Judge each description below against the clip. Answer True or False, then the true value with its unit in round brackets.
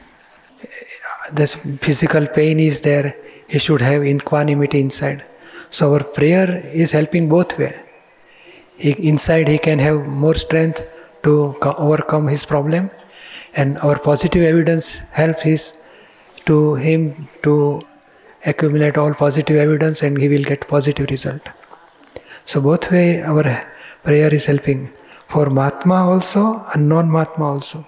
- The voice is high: False (150 Hz)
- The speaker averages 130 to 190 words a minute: True (135 wpm)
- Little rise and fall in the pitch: True (1.8 semitones)